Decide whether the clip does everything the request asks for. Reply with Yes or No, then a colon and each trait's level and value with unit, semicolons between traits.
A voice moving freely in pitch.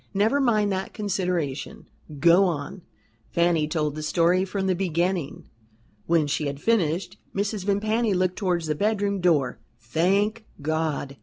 No: average, 4.4 semitones